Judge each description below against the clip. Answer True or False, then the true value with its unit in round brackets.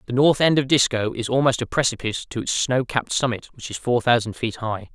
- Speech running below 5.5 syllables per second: False (5.9 syllables/s)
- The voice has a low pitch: True (120 Hz)